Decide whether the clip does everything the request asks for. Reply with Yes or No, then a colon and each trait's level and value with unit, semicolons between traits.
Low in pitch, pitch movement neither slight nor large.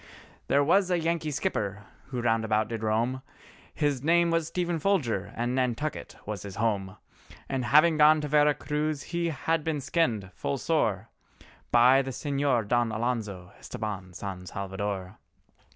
No: low, 125 Hz; wide, 6.3 semitones